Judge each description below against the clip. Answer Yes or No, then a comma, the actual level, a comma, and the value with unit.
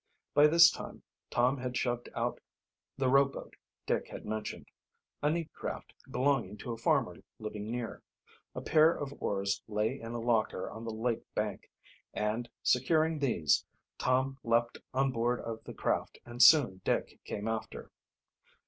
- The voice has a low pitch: Yes, low, 120 Hz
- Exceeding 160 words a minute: No, average, 155 wpm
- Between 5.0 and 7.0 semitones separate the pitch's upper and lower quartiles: No, average, 3.6 semitones